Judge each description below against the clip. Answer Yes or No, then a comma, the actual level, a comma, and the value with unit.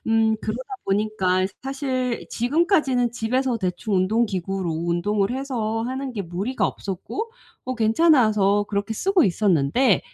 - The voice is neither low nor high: No, high, 225 Hz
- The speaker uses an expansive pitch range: No, average, 4.8 semitones